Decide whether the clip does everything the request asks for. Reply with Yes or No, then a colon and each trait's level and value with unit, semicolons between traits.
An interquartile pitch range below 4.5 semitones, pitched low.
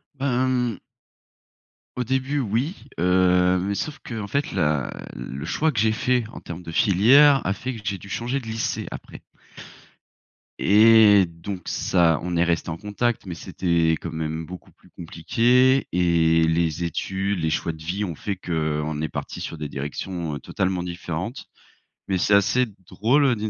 No: wide, 5.4 semitones; very low, 95 Hz